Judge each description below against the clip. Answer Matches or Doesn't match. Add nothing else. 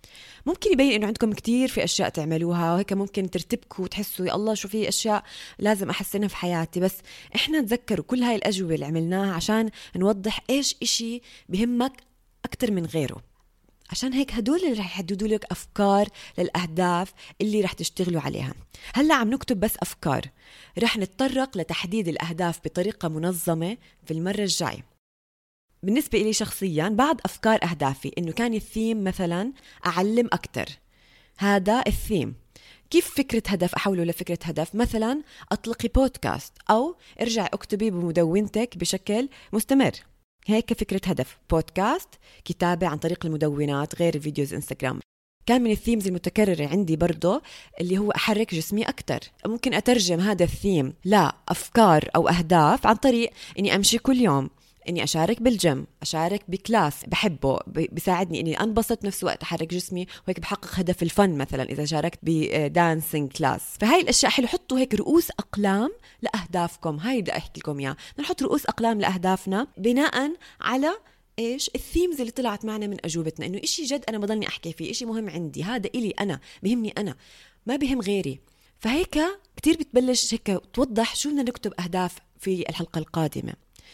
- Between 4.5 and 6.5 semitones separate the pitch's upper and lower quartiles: Matches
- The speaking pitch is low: Doesn't match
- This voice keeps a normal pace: Doesn't match